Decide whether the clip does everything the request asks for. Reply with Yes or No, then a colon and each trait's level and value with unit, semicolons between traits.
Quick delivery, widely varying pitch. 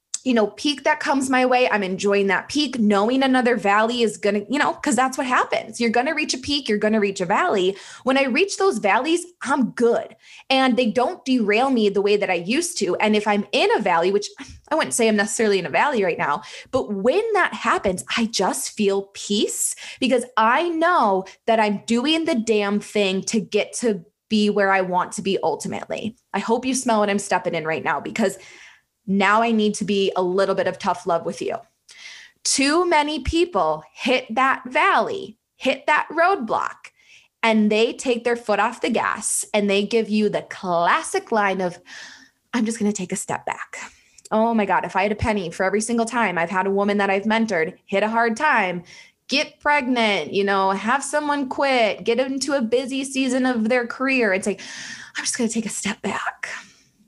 No: fast, 210 wpm; average, 4.8 semitones